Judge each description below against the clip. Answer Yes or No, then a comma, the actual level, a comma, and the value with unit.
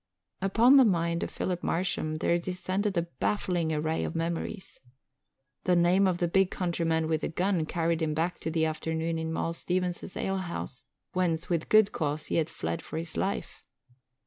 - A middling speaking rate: Yes, average, 175 wpm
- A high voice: No, medium, 170 Hz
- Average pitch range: No, narrow, 2.3 semitones